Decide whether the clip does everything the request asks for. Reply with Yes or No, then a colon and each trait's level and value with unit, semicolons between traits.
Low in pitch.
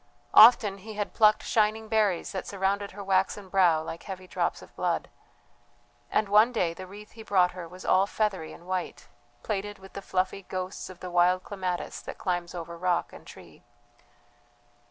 No: high, 190 Hz